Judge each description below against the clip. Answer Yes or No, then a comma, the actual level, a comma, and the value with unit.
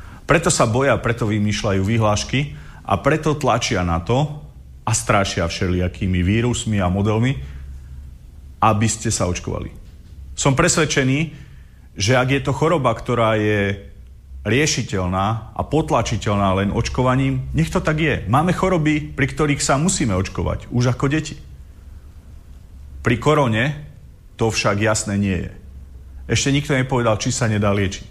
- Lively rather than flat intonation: Yes, wide, 7.1 semitones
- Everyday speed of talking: Yes, average, 135 wpm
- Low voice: Yes, low, 110 Hz